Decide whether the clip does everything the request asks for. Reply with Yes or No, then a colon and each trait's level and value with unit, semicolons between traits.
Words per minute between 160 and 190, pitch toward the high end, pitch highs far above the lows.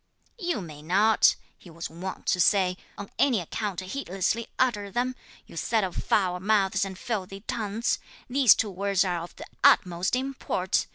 No: average, 165 wpm; high, 195 Hz; average, 3.8 semitones